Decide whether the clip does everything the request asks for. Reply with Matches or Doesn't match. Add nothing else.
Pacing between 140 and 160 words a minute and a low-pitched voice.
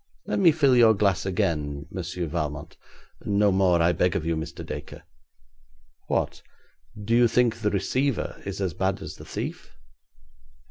Matches